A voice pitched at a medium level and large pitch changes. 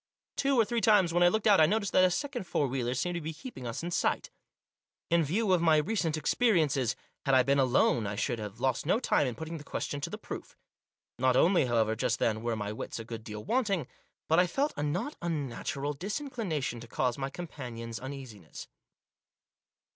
Yes: medium, 150 Hz; wide, 6.9 semitones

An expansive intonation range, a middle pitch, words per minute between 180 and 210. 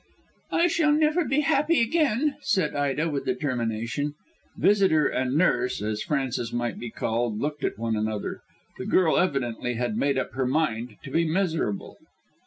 No: wide, 7.8 semitones; medium, 145 Hz; average, 160 wpm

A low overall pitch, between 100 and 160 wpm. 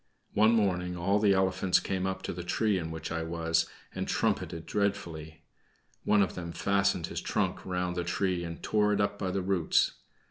No: very low, 90 Hz; average, 190 wpm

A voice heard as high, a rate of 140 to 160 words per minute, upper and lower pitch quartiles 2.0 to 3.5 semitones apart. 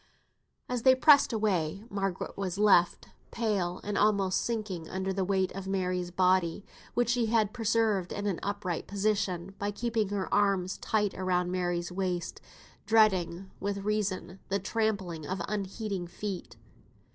Yes: high, 195 Hz; average, 145 wpm; narrow, 2.5 semitones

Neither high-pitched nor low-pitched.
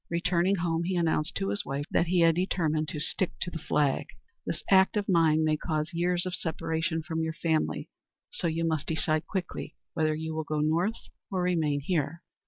Yes: medium, 165 Hz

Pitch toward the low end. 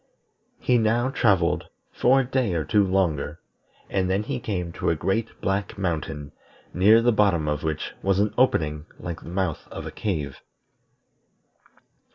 Yes: very low, 95 Hz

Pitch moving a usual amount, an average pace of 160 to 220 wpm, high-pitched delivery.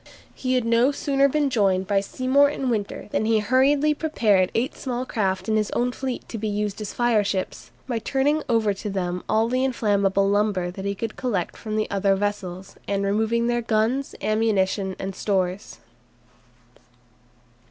Yes: average, 4.0 semitones; average, 165 wpm; high, 215 Hz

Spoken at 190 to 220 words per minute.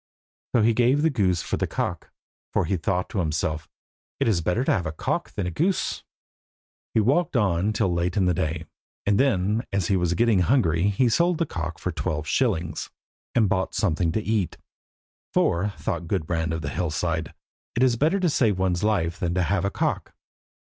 Yes: average, 195 wpm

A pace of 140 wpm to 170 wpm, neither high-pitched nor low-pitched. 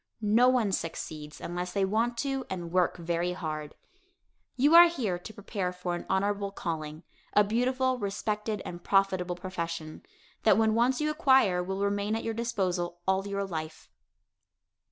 No: average, 155 wpm; high, 195 Hz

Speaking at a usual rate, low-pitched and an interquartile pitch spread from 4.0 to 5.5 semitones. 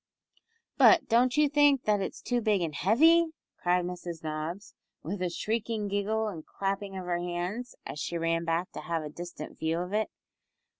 No: average, 185 wpm; high, 190 Hz; average, 4.5 semitones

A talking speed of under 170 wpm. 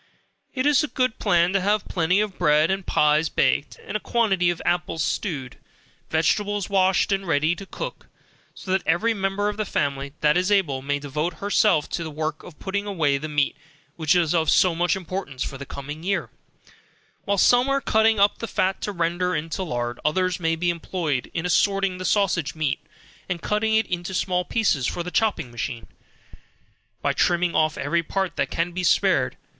No: average, 195 wpm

